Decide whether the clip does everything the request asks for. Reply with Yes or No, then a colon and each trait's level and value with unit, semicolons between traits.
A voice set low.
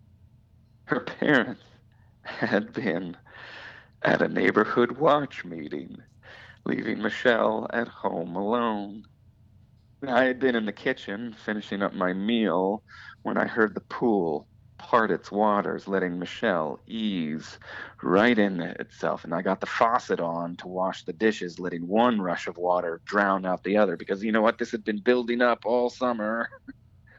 Yes: low, 105 Hz